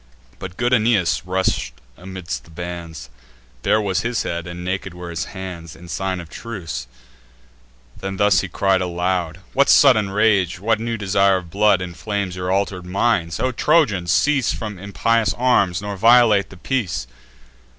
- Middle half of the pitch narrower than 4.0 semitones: Yes, average, 3.4 semitones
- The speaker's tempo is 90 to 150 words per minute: No, average, 160 wpm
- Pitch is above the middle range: No, very low, 95 Hz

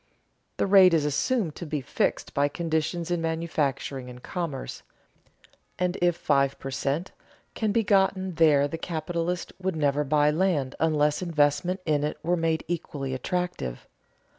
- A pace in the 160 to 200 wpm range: No, average, 150 wpm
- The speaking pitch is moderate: Yes, medium, 160 Hz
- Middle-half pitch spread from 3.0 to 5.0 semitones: Yes, average, 3.5 semitones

